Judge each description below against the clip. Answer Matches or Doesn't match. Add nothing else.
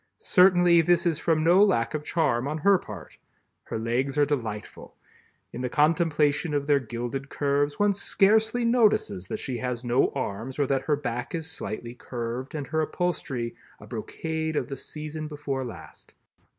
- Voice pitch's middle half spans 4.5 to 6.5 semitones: Matches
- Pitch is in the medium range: Matches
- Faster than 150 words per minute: Matches